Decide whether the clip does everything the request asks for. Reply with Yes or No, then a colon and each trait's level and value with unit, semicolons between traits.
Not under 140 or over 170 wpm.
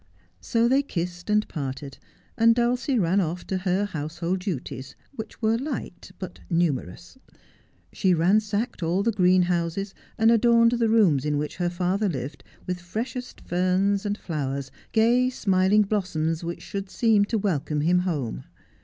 Yes: average, 155 wpm